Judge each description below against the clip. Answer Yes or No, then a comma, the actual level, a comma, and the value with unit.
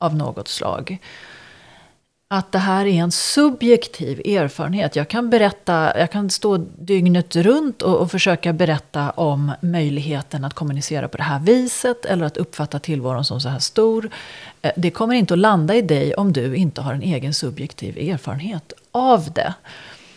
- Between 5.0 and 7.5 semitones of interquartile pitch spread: Yes, average, 5.3 semitones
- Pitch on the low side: No, medium, 170 Hz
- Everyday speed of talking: Yes, average, 165 wpm